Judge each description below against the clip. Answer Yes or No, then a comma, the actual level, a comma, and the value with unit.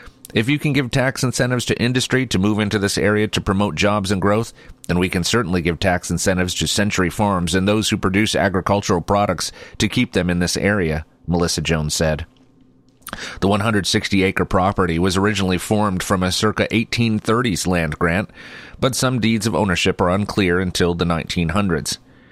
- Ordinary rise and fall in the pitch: Yes, average, 3.3 semitones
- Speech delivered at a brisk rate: No, average, 175 wpm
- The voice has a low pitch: Yes, low, 100 Hz